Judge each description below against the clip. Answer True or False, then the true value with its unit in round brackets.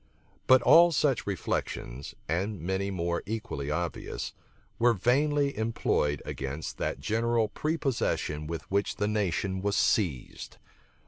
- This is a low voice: True (100 Hz)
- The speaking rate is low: True (120 wpm)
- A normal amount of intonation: False (6.0 semitones)